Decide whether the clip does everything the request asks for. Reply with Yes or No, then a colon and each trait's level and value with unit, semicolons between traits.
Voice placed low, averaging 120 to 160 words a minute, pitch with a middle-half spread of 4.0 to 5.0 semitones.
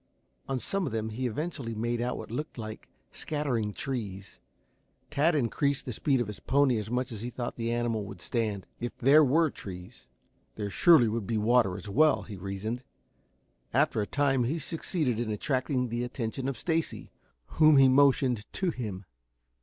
No: low, 120 Hz; average, 175 wpm; average, 4.5 semitones